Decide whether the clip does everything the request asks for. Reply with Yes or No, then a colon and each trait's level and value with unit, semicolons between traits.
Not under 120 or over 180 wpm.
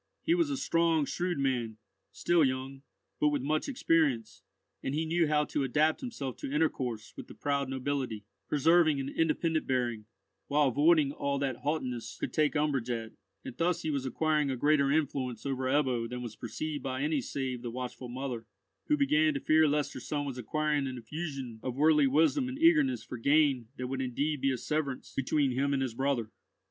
No: average, 195 wpm